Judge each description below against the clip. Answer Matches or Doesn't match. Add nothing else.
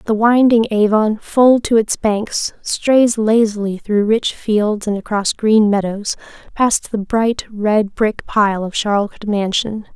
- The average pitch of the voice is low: Doesn't match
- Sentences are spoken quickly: Doesn't match